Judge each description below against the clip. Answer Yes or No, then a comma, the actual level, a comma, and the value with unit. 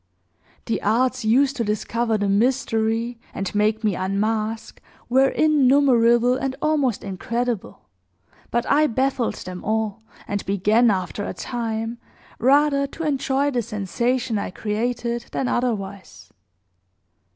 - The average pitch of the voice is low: No, high, 235 Hz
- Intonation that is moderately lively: Yes, average, 3.5 semitones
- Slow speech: Yes, slow, 120 wpm